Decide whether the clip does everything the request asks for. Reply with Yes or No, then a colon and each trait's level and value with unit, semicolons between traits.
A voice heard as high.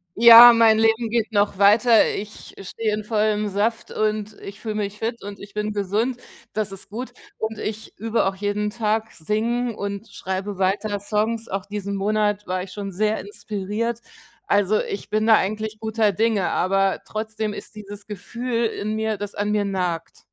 Yes: high, 210 Hz